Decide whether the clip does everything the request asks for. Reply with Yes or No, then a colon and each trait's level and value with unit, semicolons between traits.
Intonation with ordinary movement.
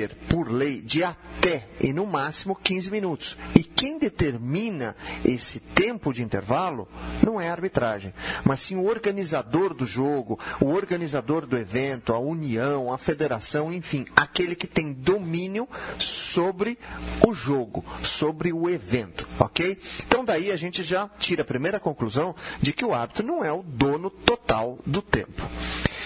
No: wide, 6.0 semitones